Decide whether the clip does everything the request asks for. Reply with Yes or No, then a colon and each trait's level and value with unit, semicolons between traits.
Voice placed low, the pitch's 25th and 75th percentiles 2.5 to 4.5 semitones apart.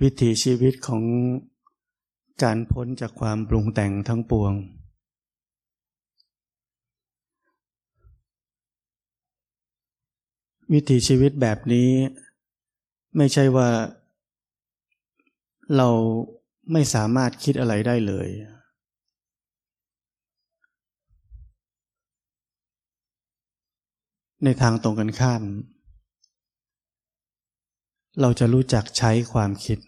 Yes: low, 120 Hz; average, 3.1 semitones